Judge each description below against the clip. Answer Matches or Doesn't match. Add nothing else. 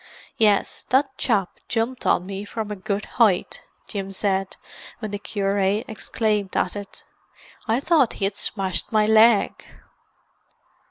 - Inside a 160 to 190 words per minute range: Doesn't match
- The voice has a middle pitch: Doesn't match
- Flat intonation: Matches